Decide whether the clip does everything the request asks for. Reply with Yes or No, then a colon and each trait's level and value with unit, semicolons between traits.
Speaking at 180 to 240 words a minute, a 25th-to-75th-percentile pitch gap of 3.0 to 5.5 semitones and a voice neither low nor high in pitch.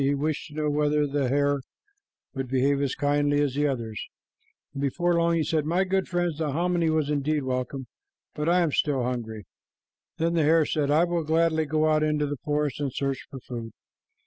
No: average, 200 wpm; narrow, 2.5 semitones; medium, 150 Hz